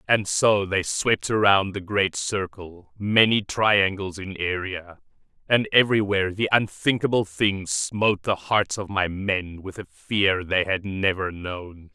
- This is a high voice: No, very low, 95 Hz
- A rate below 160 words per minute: Yes, average, 150 wpm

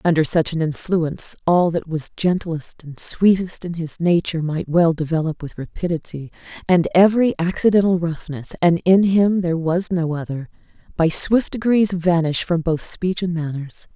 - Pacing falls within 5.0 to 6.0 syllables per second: No, 4.8 syllables/s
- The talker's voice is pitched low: No, medium, 170 Hz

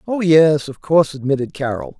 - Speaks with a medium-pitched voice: Yes, medium, 150 Hz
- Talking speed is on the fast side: No, average, 180 wpm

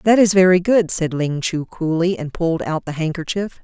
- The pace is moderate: No, fast, 215 wpm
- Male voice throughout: No, female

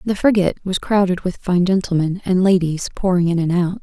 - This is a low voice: No, medium, 185 Hz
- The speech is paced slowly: No, fast, 205 wpm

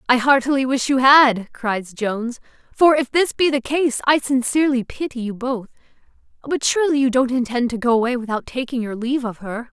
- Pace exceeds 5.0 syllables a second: Yes, 5.4 syllables/s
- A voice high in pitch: Yes, very high, 255 Hz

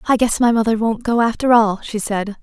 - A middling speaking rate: No, fast, 245 wpm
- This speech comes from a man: No, female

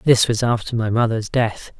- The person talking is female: No, male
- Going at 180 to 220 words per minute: Yes, average, 200 wpm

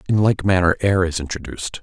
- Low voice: Yes, very low, 90 Hz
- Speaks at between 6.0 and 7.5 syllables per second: Yes, 6.1 syllables/s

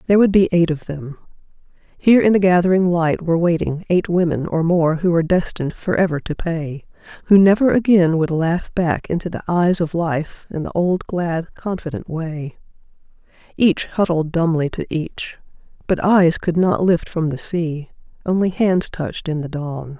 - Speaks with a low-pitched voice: No, medium, 170 Hz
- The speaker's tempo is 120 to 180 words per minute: Yes, average, 175 wpm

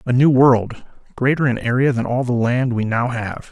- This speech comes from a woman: No, male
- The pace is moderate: No, fast, 220 wpm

